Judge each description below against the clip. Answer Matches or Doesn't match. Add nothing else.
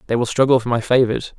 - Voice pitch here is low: Matches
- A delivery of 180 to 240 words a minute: Doesn't match